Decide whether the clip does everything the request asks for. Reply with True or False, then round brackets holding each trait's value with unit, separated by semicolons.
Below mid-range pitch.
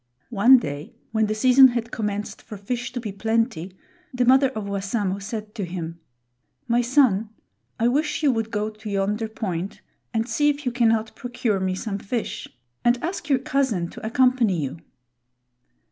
False (225 Hz)